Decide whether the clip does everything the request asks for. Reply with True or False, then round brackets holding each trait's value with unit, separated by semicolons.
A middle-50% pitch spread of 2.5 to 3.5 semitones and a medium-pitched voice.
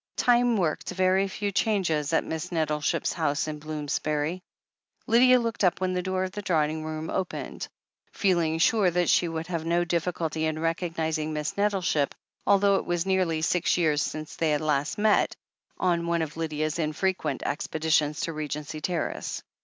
True (3.2 semitones; 165 Hz)